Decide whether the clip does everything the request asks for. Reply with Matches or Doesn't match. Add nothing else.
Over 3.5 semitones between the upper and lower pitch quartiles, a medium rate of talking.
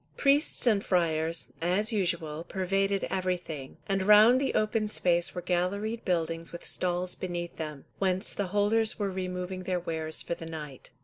Doesn't match